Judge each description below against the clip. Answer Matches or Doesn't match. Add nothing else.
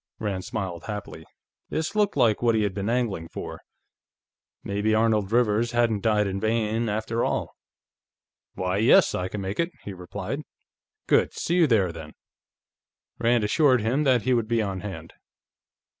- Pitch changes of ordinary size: Matches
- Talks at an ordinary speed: Matches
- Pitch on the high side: Doesn't match